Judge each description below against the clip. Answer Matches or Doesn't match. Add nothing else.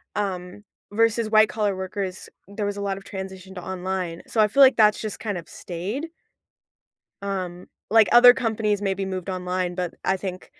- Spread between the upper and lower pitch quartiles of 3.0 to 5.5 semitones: Doesn't match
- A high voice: Matches